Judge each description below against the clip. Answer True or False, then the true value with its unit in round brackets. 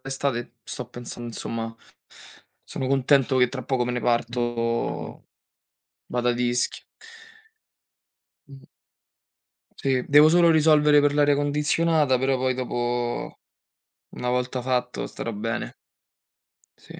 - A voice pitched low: True (125 Hz)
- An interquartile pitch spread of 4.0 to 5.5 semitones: False (2.8 semitones)